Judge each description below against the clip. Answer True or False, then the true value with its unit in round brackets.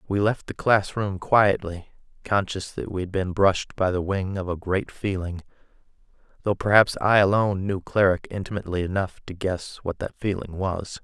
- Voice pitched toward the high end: False (95 Hz)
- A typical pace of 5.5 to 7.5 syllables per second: False (5.0 syllables/s)